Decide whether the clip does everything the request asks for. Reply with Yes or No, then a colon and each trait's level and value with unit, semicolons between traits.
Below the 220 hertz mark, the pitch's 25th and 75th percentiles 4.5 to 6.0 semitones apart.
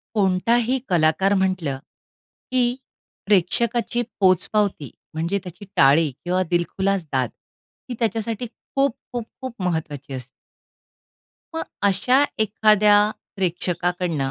Yes: high, 190 Hz; average, 4.8 semitones